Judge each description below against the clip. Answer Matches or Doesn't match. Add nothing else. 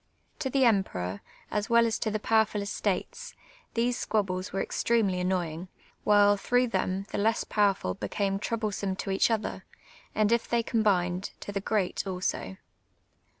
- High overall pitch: Matches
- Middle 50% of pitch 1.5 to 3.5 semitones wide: Matches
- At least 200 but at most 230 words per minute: Doesn't match